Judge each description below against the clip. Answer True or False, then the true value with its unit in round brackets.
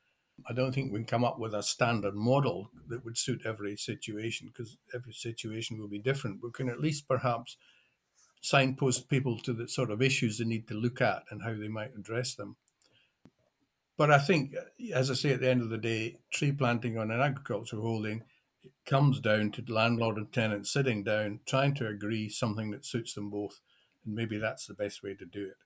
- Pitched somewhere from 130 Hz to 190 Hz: False (115 Hz)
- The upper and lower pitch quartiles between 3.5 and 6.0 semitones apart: False (3.1 semitones)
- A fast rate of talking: True (210 wpm)